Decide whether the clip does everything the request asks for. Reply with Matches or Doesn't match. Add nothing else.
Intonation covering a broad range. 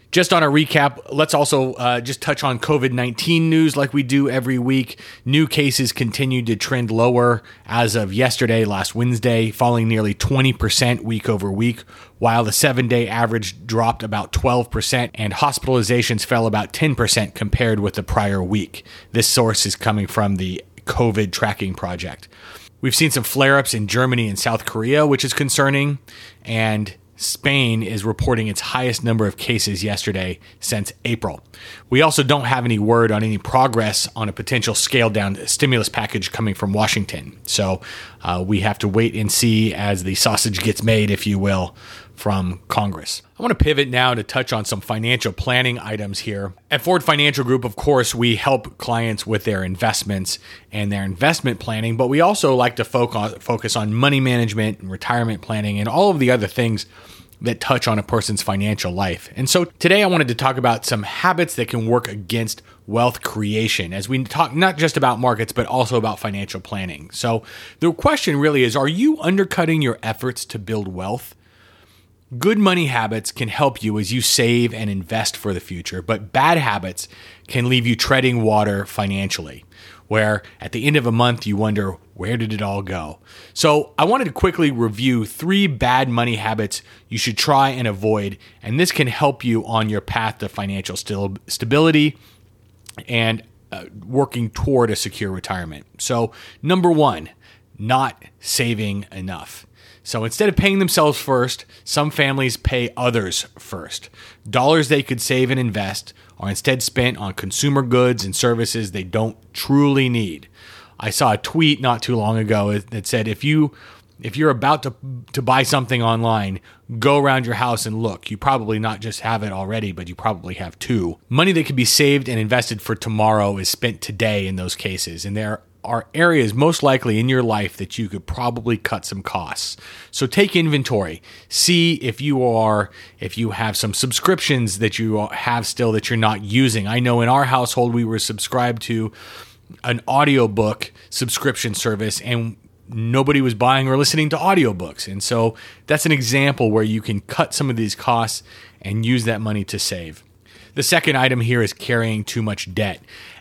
Doesn't match